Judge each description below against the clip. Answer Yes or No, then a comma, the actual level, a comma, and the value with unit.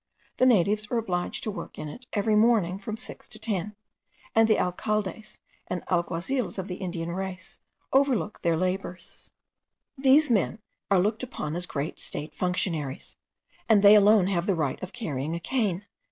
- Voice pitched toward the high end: Yes, high, 195 Hz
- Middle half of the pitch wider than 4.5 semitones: No, average, 3.7 semitones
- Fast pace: No, average, 165 wpm